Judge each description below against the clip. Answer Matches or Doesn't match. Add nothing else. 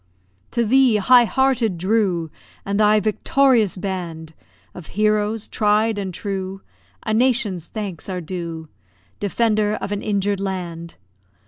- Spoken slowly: Matches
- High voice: Matches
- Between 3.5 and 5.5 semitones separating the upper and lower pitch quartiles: Doesn't match